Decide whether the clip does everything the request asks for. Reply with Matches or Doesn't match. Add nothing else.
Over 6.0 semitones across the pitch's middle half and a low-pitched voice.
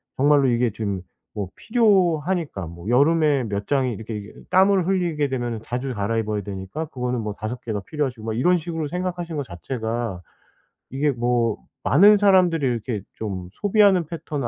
Matches